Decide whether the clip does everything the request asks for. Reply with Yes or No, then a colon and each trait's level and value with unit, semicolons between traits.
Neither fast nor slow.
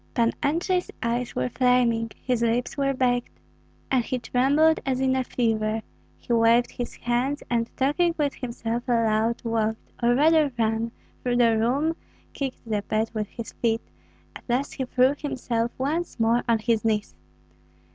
Yes: average, 160 wpm